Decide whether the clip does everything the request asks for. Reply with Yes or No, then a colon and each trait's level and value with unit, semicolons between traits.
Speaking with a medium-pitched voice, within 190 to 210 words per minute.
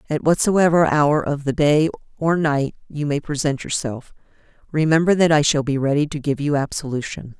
No: medium, 150 Hz; average, 180 wpm